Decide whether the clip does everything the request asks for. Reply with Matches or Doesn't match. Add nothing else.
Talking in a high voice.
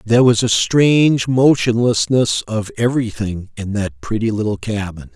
Doesn't match